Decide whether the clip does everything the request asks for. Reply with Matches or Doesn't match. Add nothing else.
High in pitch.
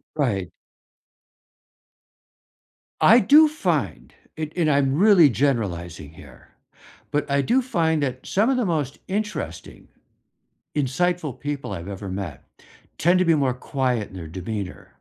Doesn't match